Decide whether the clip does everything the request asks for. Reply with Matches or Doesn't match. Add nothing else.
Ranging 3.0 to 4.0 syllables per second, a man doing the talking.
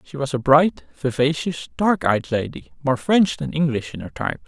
Doesn't match